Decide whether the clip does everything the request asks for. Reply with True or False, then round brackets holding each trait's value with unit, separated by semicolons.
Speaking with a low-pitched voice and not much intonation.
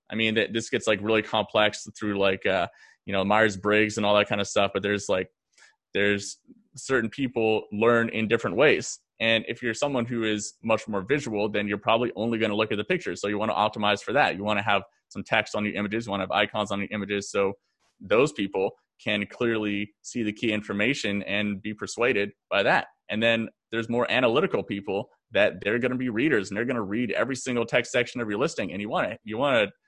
True (110 Hz; 2.0 semitones)